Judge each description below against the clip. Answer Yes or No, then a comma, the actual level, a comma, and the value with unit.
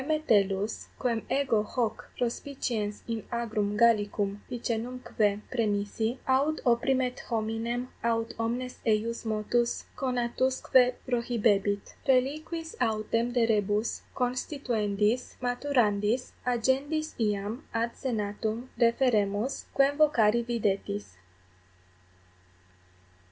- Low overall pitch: No, high, 235 Hz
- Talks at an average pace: No, slow, 85 wpm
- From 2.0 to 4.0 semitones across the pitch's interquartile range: Yes, average, 3.1 semitones